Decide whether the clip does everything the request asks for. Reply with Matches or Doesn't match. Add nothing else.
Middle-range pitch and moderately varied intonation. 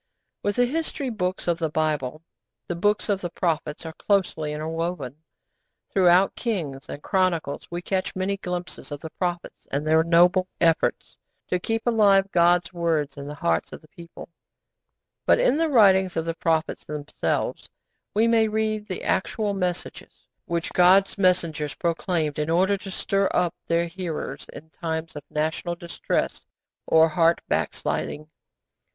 Matches